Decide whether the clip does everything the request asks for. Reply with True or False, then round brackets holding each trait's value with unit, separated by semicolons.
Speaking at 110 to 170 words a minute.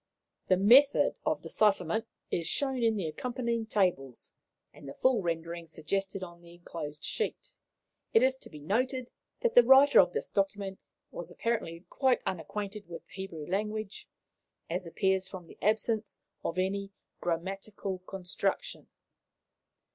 True (140 wpm)